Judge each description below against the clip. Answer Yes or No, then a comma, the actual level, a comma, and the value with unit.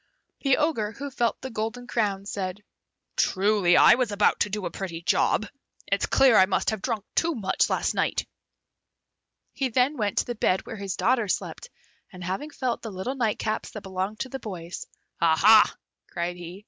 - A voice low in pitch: No, high, 210 Hz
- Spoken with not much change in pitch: No, average, 4.6 semitones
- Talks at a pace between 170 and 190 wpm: Yes, average, 185 wpm